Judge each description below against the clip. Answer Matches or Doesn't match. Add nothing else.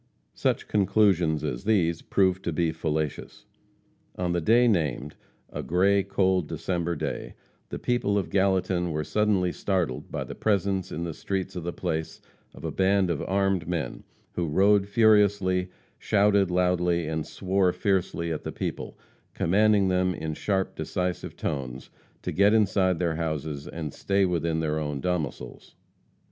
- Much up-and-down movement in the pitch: Doesn't match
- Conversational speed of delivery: Matches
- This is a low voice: Matches